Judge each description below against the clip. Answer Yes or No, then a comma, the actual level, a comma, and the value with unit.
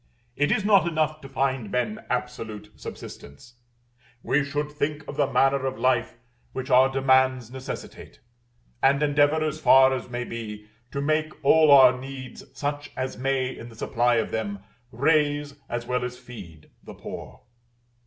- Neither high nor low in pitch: No, low, 130 Hz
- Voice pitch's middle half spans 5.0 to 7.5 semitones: No, average, 3.0 semitones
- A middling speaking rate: Yes, average, 160 wpm